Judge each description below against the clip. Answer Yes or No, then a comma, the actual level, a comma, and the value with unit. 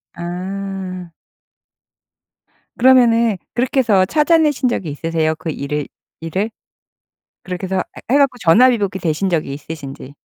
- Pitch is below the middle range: No, high, 190 Hz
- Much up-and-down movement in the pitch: Yes, wide, 6.4 semitones